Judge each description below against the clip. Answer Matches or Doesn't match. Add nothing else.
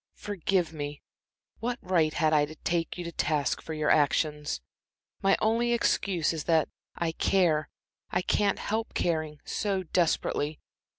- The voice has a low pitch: Doesn't match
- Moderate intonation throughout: Matches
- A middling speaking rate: Matches